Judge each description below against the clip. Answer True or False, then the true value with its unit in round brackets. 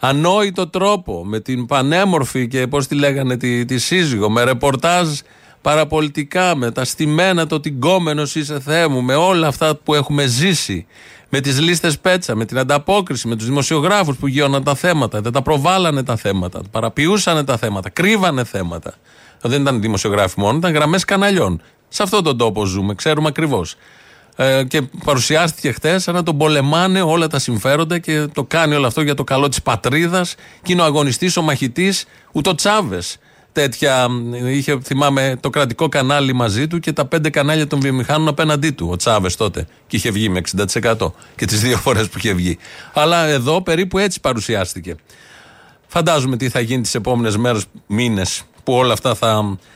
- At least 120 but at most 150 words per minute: False (170 wpm)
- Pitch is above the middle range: False (140 Hz)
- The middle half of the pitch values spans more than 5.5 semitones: False (5.1 semitones)